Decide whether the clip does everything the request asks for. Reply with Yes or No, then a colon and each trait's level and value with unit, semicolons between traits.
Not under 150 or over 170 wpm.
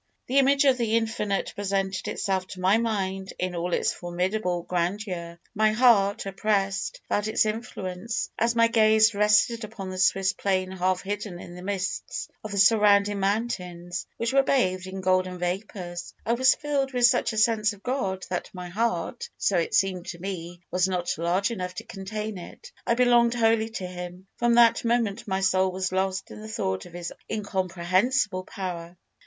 No: average, 180 wpm